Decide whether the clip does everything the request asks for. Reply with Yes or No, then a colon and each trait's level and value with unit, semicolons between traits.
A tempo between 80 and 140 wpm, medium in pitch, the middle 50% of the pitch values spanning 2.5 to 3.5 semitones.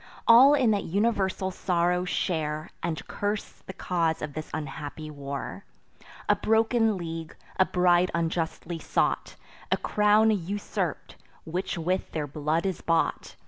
No: slow, 135 wpm; medium, 175 Hz; average, 4.0 semitones